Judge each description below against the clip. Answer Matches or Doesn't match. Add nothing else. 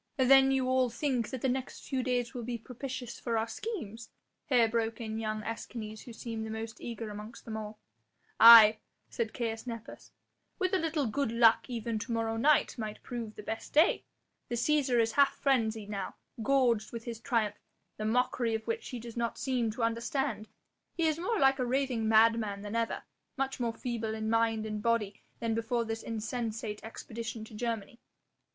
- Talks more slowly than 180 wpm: Doesn't match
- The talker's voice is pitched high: Matches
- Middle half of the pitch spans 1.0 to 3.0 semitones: Matches